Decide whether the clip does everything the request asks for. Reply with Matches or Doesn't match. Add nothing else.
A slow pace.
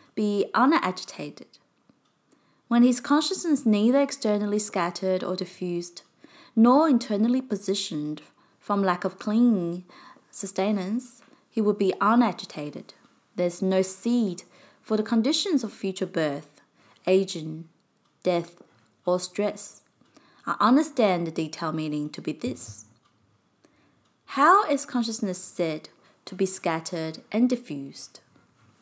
Matches